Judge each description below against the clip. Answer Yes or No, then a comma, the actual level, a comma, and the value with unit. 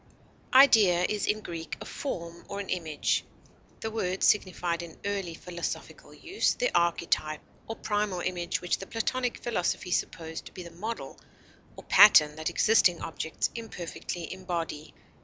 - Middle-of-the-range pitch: Yes, medium, 180 Hz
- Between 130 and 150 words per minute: Yes, average, 145 wpm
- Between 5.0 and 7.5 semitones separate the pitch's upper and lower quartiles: No, average, 3.8 semitones